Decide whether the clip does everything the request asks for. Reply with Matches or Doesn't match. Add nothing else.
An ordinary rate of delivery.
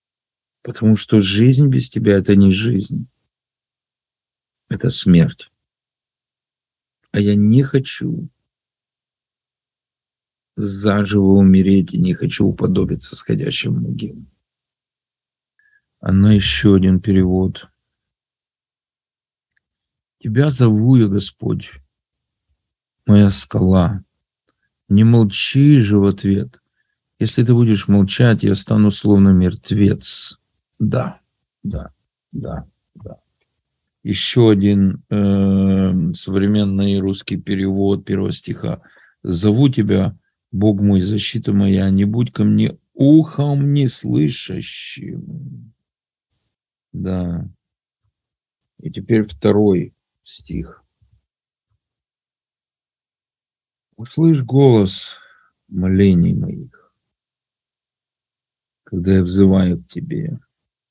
Doesn't match